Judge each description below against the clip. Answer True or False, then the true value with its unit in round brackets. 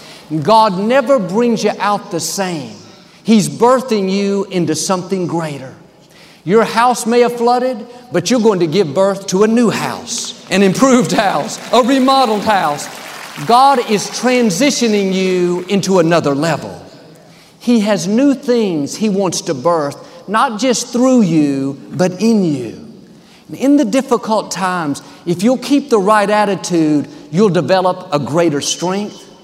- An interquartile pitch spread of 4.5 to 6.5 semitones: True (5.0 semitones)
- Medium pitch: False (200 Hz)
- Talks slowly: False (145 wpm)